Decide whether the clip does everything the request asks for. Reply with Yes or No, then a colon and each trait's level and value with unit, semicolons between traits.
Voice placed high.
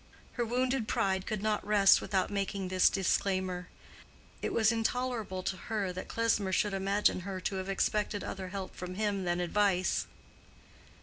Yes: high, 195 Hz